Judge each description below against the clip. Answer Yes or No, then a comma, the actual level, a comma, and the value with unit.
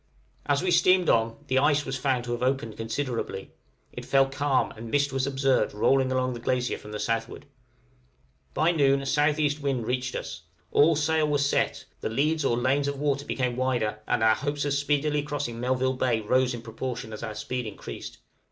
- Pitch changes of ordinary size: Yes, average, 3.1 semitones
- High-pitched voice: No, low, 130 Hz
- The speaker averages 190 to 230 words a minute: Yes, average, 195 wpm